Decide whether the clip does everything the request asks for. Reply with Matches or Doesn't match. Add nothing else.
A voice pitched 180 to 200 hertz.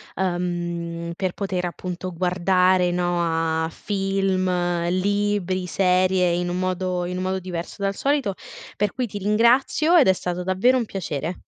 Matches